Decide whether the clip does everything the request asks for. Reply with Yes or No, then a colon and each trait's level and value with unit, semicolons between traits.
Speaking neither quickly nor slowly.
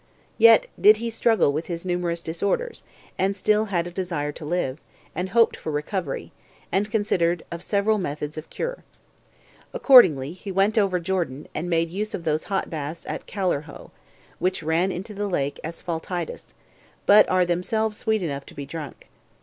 Yes: average, 165 wpm